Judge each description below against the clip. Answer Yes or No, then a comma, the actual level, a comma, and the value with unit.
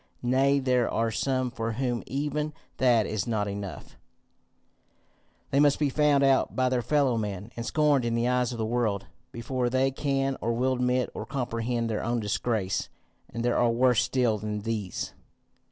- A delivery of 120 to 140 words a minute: No, average, 175 wpm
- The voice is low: Yes, low, 120 Hz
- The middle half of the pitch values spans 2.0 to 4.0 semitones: Yes, average, 2.7 semitones